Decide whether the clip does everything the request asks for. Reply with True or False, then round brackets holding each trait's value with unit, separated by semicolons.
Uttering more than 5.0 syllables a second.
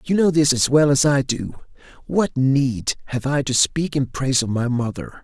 False (4.6 syllables/s)